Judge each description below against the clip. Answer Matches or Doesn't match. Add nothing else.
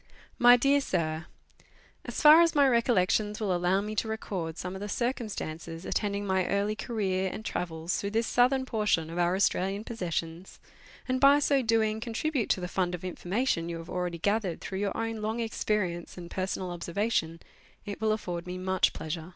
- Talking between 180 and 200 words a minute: Matches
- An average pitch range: Matches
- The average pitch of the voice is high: Matches